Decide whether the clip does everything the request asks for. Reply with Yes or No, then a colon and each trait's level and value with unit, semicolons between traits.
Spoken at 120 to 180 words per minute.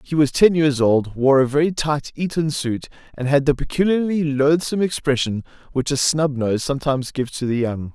No: average, 195 wpm